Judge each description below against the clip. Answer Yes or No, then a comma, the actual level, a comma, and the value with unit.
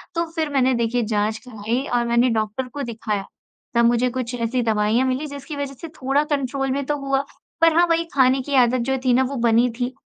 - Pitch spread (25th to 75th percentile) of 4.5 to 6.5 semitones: No, average, 2.9 semitones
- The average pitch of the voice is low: No, very high, 255 Hz